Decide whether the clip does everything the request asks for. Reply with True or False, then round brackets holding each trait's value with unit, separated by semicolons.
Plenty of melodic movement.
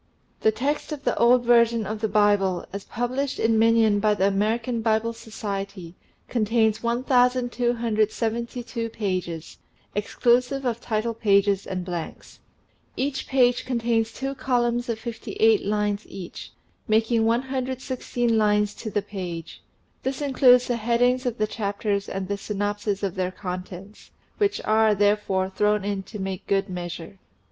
False (3.1 semitones)